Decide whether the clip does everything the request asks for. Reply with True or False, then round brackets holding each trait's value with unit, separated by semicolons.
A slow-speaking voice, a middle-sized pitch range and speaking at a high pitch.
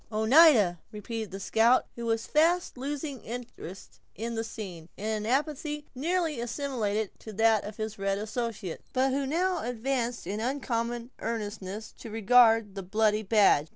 False (155 wpm; 3.8 semitones; 230 Hz)